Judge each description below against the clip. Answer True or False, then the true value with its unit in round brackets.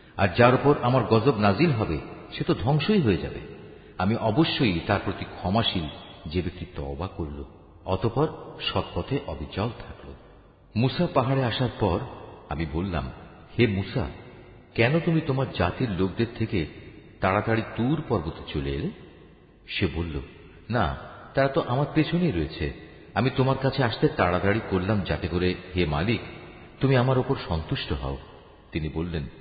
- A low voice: True (100 Hz)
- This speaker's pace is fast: True (140 wpm)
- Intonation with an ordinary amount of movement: False (7.1 semitones)